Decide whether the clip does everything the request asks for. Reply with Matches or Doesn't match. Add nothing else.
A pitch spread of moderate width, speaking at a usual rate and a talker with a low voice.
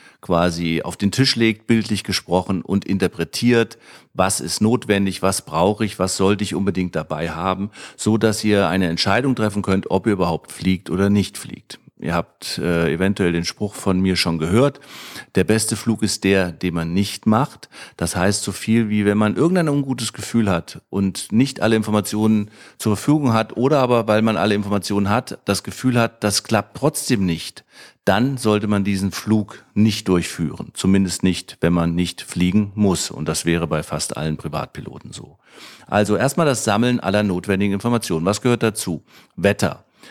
Matches